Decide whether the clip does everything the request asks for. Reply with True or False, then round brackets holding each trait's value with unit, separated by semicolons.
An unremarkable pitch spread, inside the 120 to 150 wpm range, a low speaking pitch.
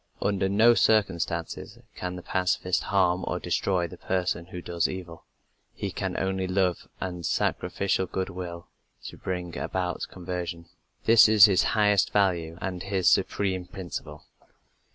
False (1.7 semitones; 140 wpm; 90 Hz)